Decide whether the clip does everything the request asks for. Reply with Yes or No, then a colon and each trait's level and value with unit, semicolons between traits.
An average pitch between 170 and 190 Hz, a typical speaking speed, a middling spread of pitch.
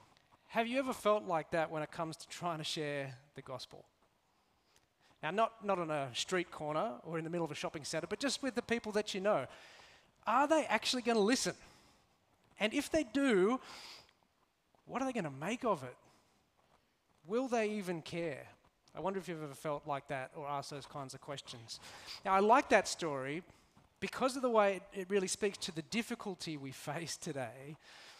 No: medium, 185 Hz; average, 195 wpm; wide, 6.4 semitones